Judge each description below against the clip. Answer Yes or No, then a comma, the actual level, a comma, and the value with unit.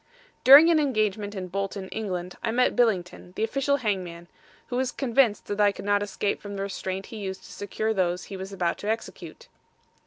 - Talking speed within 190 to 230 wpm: Yes, average, 195 wpm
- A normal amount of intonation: Yes, average, 3.3 semitones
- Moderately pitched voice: No, high, 205 Hz